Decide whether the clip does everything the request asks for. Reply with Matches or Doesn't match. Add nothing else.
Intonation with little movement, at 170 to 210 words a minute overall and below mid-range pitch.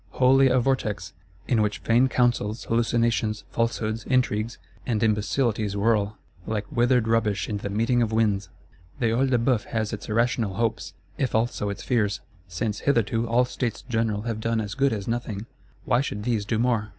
Matches